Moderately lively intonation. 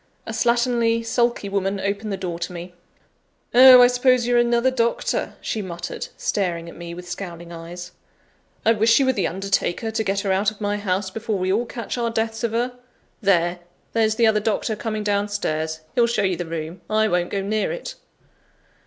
Yes: average, 4.3 semitones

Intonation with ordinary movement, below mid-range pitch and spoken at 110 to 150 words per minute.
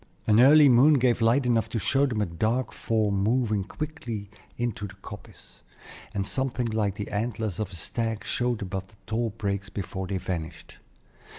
No: average, 3.3 semitones; low, 110 Hz; average, 175 wpm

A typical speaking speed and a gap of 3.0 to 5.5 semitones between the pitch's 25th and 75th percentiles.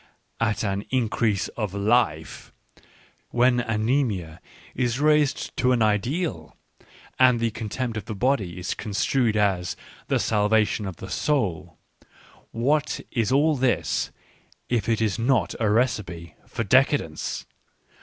No: slow, 130 wpm; average, 4.1 semitones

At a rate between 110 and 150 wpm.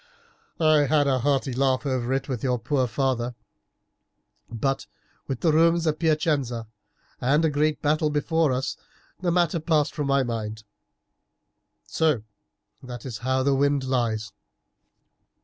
Yes: average, 140 wpm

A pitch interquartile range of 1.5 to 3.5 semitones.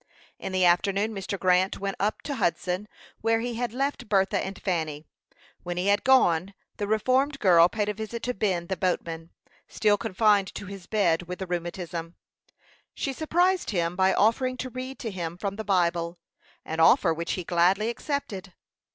No: average, 4.0 semitones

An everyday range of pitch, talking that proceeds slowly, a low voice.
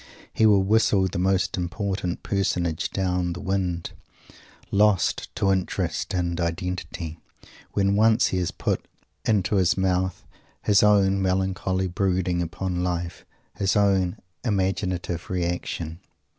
No: narrow, 1.9 semitones; slow, 120 wpm; very low, 95 Hz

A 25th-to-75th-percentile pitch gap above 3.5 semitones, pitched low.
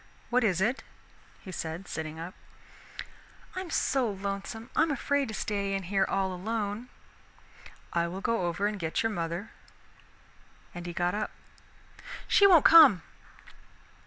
No: average, 4.6 semitones; high, 200 Hz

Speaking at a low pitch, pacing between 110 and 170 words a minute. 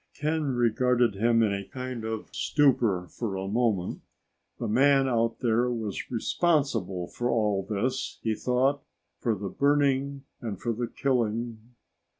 Yes: low, 120 Hz; average, 145 wpm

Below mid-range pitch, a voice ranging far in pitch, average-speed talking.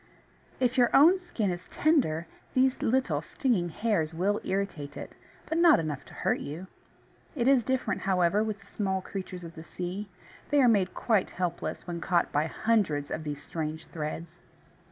No: high, 190 Hz; wide, 6.3 semitones; average, 175 wpm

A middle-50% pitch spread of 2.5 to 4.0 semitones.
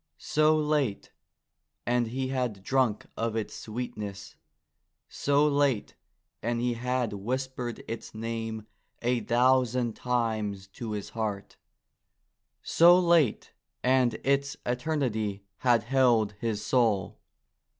Yes: average, 3.2 semitones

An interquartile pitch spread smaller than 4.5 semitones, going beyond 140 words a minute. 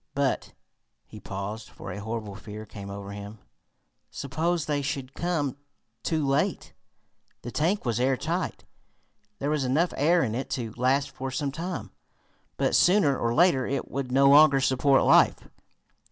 No: average, 4.8 semitones; average, 155 wpm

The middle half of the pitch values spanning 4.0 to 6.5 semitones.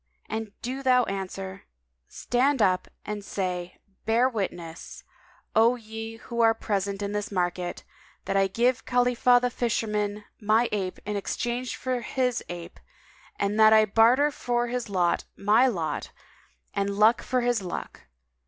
No: average, 3.6 semitones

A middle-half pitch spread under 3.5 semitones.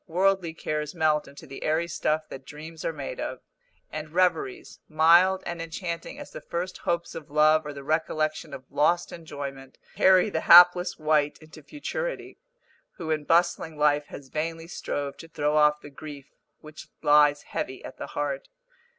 Yes: narrow, 2.5 semitones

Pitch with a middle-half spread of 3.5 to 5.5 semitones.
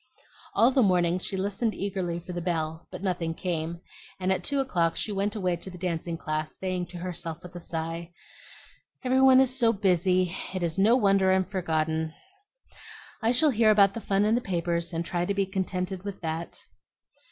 No: average, 2.9 semitones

